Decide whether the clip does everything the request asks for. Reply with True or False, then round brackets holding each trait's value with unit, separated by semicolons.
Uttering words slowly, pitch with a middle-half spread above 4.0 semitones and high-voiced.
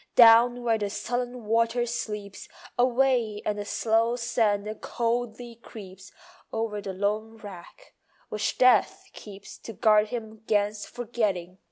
False (130 wpm; 2.5 semitones; 220 Hz)